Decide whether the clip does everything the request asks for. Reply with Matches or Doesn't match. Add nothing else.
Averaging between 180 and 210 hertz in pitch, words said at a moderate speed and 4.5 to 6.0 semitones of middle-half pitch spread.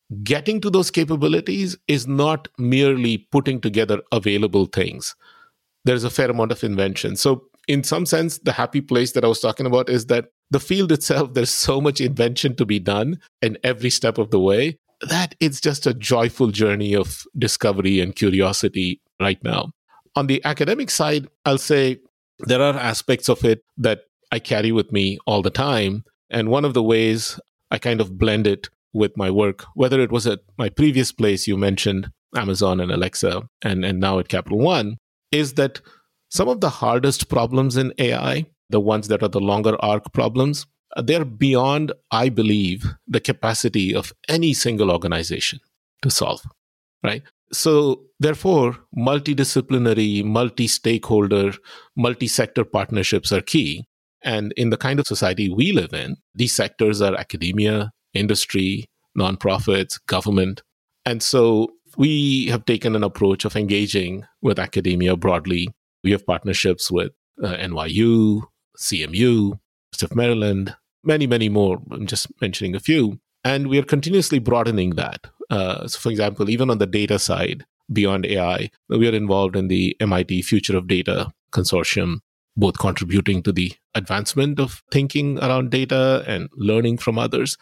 Doesn't match